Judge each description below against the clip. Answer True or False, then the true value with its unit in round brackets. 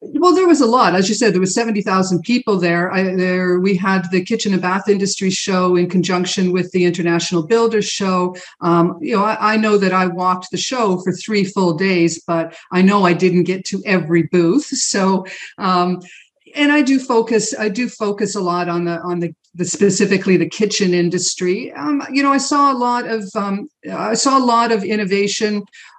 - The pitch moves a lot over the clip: False (3.4 semitones)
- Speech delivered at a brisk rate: True (210 wpm)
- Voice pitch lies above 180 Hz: True (190 Hz)